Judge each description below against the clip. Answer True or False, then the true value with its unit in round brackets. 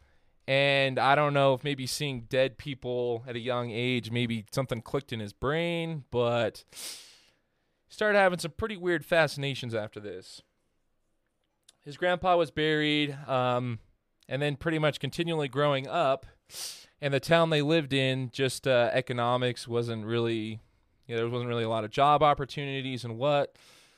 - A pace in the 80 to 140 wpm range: False (160 wpm)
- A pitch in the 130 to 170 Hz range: True (135 Hz)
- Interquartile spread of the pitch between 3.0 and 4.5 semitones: True (3.7 semitones)